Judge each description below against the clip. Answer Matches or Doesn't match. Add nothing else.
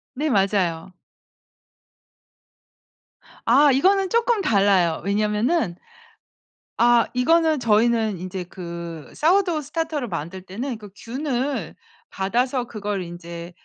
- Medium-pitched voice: Doesn't match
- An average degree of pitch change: Doesn't match